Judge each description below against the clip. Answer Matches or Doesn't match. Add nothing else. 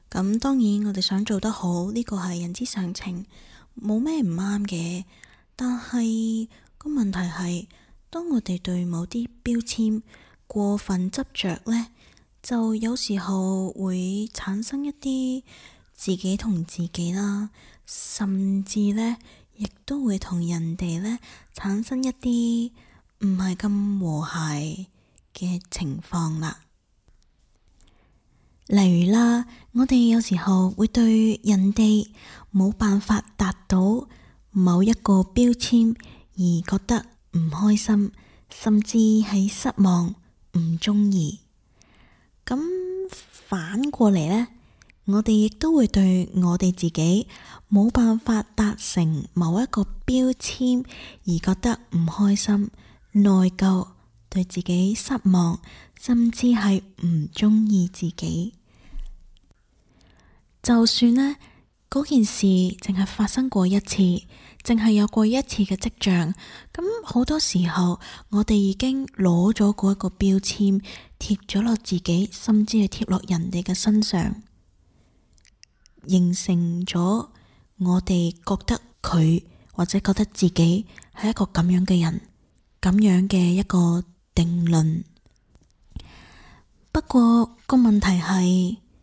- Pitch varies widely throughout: Doesn't match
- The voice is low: Doesn't match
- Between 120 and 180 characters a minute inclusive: Matches